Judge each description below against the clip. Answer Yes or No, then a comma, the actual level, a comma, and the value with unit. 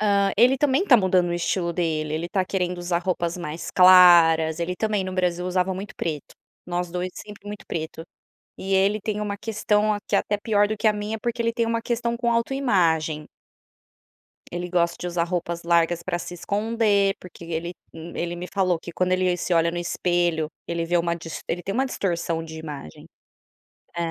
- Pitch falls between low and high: Yes, medium, 180 Hz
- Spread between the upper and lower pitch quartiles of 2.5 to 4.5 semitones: Yes, average, 3.4 semitones